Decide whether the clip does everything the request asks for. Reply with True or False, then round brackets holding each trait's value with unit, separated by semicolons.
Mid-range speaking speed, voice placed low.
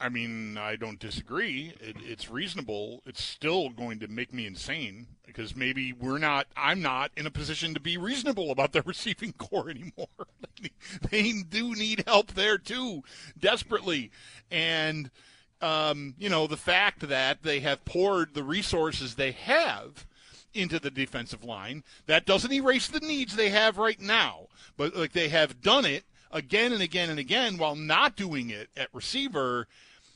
False (165 wpm; 155 Hz)